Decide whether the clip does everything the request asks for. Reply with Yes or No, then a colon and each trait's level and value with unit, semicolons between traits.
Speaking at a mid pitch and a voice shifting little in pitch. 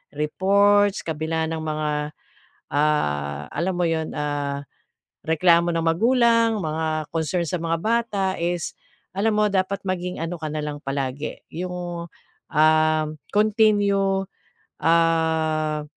No: medium, 165 Hz; average, 3.8 semitones